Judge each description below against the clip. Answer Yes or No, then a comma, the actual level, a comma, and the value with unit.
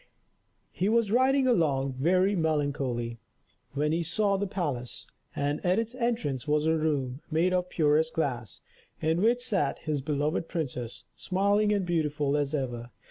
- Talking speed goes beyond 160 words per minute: No, average, 155 wpm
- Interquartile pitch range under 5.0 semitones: No, wide, 5.4 semitones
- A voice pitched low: No, medium, 155 Hz